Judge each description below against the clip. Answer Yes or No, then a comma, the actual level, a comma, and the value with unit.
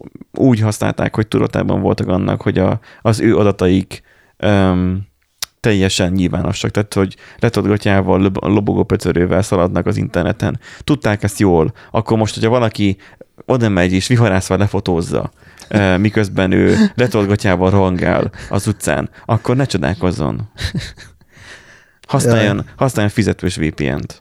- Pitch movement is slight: No, average, 3.0 semitones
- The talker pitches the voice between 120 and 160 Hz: No, low, 100 Hz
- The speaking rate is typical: Yes, average, 120 wpm